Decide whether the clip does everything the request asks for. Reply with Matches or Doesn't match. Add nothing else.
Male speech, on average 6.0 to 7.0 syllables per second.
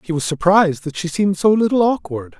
Matches